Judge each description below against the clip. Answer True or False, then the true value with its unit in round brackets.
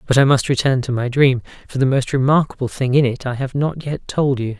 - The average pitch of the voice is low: True (130 Hz)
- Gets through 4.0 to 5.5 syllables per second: False (5.7 syllables/s)